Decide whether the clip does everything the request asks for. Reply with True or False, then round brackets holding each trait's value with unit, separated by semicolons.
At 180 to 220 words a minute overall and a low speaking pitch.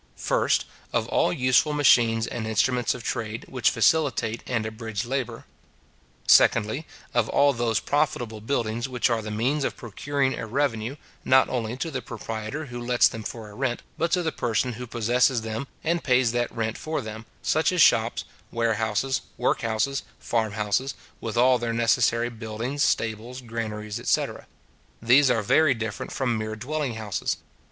False (165 wpm; 120 Hz)